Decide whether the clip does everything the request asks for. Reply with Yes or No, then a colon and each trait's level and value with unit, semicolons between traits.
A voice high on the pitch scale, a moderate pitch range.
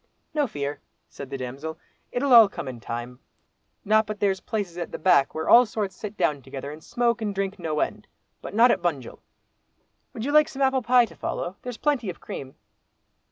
No: high, 195 Hz; wide, 8.0 semitones